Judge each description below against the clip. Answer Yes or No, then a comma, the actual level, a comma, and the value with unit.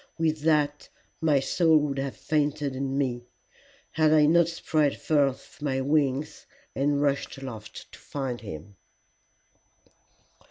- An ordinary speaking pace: No, slow, 125 wpm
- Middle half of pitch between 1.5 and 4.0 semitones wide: Yes, narrow, 2.4 semitones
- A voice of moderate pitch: Yes, medium, 145 Hz